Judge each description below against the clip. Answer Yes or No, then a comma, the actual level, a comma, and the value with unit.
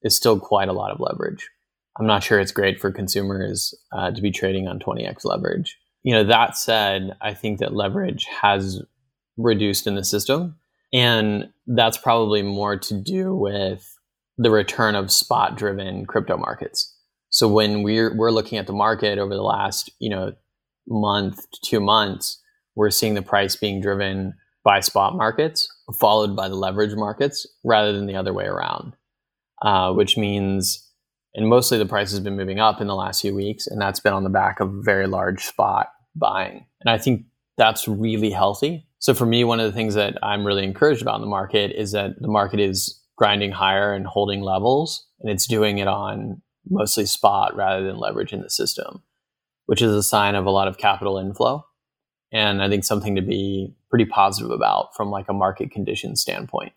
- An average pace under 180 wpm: No, average, 190 wpm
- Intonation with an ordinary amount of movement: No, narrow, 2.1 semitones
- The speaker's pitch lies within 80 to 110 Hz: Yes, low, 105 Hz